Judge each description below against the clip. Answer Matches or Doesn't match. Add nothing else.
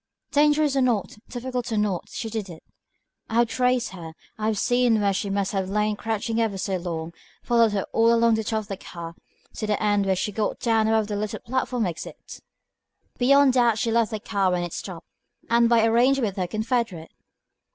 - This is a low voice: Doesn't match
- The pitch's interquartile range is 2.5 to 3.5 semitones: Matches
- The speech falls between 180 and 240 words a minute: Matches